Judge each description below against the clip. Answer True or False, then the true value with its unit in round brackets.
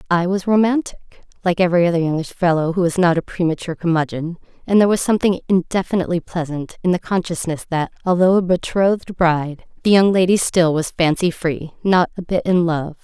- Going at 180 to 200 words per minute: True (185 wpm)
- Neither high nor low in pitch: True (175 Hz)